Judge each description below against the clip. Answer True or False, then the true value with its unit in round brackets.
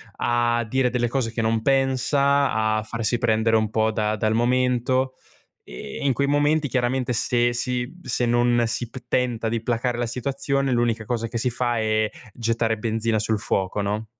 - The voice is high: False (120 Hz)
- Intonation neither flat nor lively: False (2.3 semitones)